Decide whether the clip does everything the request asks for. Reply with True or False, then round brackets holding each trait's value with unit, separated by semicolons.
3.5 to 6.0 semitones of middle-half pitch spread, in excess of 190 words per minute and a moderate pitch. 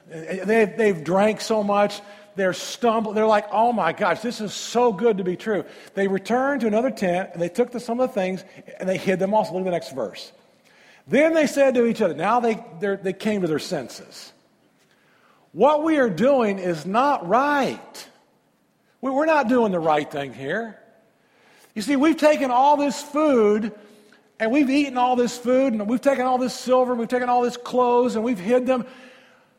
False (4.1 semitones; 200 wpm; 225 Hz)